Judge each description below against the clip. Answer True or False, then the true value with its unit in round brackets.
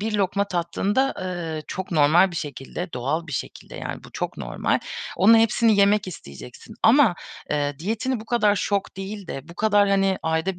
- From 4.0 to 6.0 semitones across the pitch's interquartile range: True (4.5 semitones)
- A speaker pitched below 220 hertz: True (190 Hz)